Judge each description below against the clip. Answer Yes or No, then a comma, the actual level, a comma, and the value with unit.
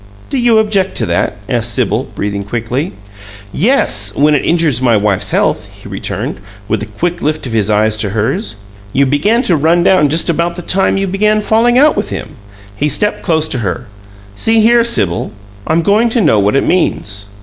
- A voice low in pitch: No, medium, 155 Hz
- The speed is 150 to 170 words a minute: No, average, 195 wpm